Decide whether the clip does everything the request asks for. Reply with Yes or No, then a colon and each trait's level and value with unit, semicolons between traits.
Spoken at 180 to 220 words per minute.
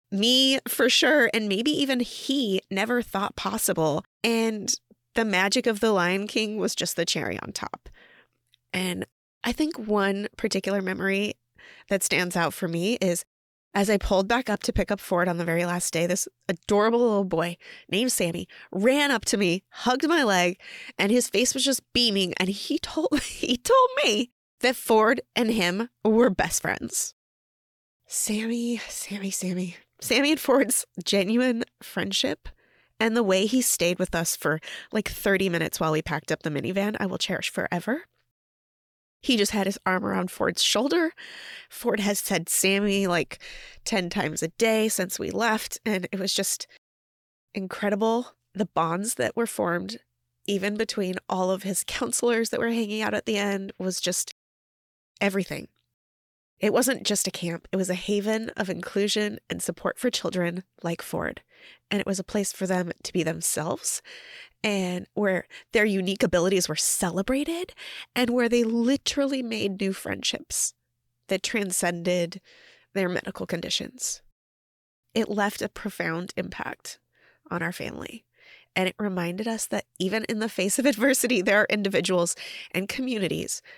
No: average, 160 wpm